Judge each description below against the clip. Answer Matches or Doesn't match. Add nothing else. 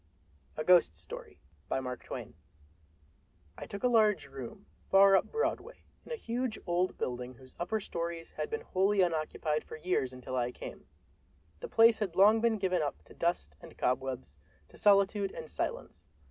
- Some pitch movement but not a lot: Doesn't match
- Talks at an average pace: Matches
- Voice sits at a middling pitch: Matches